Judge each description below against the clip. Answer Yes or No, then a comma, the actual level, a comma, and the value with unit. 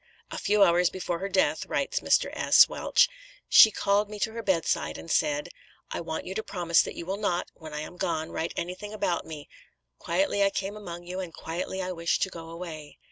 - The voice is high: No, medium, 180 Hz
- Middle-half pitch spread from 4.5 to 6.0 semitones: No, average, 3.1 semitones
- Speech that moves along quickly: Yes, fast, 215 wpm